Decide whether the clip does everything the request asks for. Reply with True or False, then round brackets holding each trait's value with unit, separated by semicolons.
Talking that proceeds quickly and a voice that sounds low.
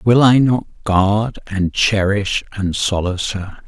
False (145 wpm; 105 Hz)